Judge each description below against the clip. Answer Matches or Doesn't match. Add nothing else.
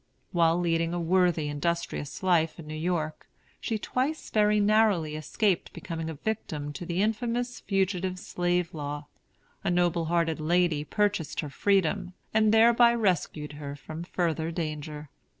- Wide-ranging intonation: Doesn't match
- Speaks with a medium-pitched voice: Matches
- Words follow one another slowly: Doesn't match